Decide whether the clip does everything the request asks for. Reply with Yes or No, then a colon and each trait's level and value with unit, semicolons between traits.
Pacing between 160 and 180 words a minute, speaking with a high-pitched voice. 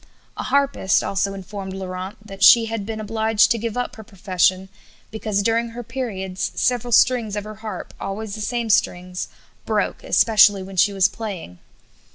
Yes: average, 170 wpm; high, 210 Hz